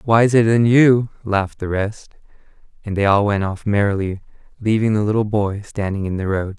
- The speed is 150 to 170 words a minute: No, average, 180 wpm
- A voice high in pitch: No, low, 105 Hz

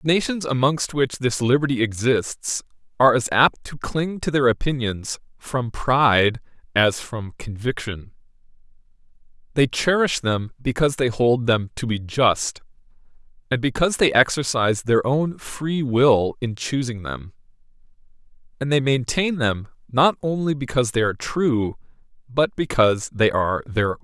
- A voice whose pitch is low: Yes, low, 125 Hz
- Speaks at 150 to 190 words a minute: No, average, 140 wpm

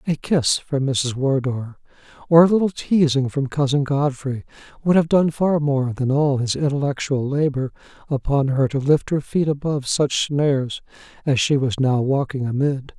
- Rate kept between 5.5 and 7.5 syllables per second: No, 4.7 syllables/s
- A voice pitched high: No, medium, 140 Hz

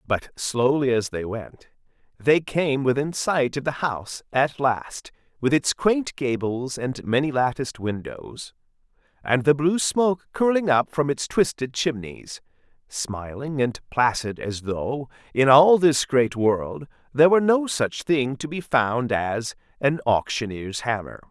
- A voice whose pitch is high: No, low, 135 Hz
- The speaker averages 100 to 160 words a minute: Yes, average, 145 wpm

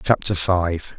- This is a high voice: No, very low, 90 Hz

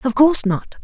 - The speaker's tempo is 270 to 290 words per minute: No, fast, 215 wpm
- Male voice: No, female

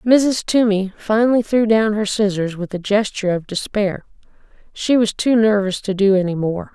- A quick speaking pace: No, average, 180 wpm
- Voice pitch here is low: No, high, 210 Hz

